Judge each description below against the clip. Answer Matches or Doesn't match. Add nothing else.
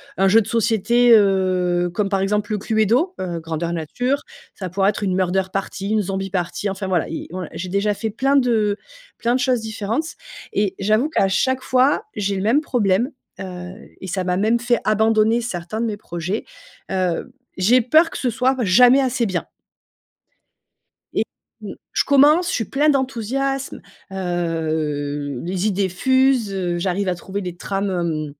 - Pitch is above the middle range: Matches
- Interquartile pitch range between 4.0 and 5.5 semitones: Matches